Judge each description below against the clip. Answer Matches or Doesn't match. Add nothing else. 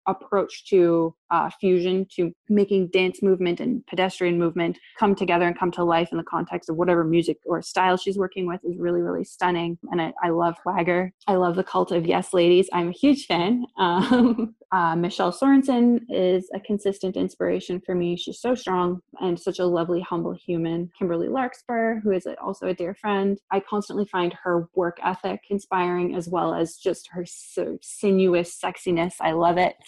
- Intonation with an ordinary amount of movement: Doesn't match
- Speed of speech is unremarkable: Matches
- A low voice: Doesn't match